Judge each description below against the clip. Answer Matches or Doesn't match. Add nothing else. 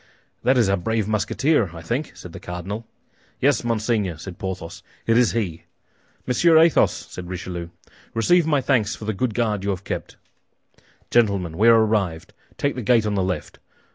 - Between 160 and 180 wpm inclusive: Matches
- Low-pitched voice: Matches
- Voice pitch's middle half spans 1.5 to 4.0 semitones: Doesn't match